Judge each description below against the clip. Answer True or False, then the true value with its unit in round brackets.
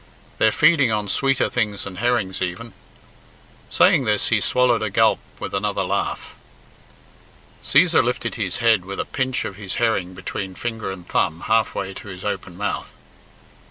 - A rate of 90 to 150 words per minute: False (160 wpm)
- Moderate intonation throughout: True (4.0 semitones)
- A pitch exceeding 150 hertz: False (110 Hz)